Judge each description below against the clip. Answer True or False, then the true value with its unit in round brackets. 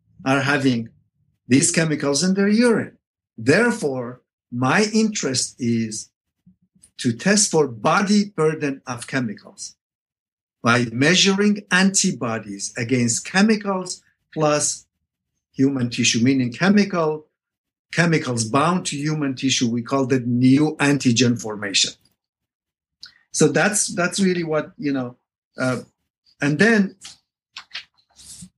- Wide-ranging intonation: True (6.6 semitones)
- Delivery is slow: True (105 wpm)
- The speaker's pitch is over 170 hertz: False (145 Hz)